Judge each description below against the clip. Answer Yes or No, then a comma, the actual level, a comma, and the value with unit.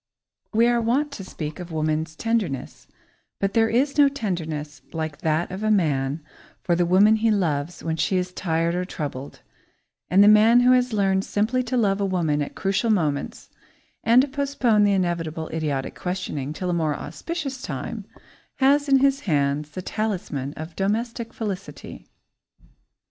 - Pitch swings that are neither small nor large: No, wide, 6.3 semitones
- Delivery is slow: No, average, 165 wpm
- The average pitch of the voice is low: No, high, 190 Hz